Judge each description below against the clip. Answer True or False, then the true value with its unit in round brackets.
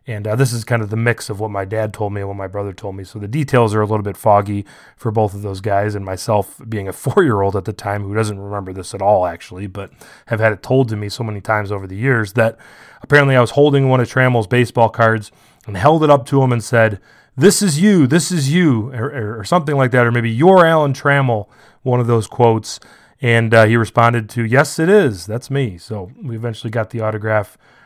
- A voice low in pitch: True (115 Hz)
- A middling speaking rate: False (250 wpm)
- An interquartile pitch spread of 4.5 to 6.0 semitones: False (3.8 semitones)